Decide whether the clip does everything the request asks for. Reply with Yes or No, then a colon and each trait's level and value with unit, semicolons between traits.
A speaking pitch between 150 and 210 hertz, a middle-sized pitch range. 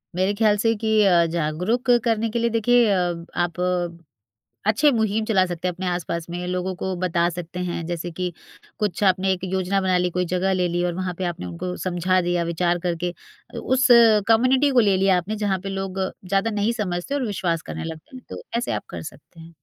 Yes: medium, 185 Hz; average, 3.3 semitones